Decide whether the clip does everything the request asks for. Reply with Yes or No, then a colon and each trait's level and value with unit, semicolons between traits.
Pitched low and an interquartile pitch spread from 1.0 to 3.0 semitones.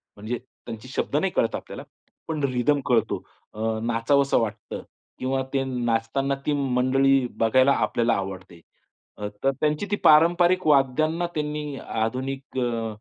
No: low, 130 Hz; average, 4.1 semitones